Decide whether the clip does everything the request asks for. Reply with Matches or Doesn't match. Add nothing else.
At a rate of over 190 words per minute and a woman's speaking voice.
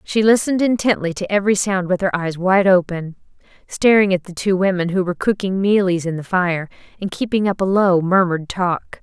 Matches